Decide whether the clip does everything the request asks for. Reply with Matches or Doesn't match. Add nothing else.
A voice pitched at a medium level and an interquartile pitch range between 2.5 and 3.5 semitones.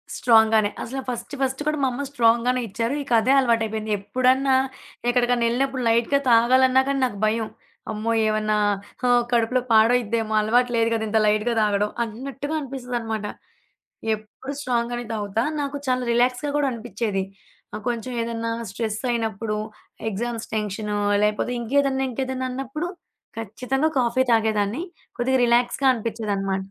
Doesn't match